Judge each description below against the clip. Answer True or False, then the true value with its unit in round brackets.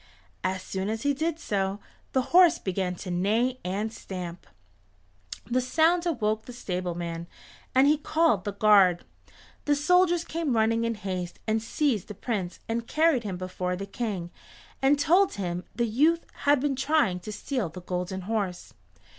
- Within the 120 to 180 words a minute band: True (165 wpm)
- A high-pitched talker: True (220 Hz)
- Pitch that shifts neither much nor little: False (7.5 semitones)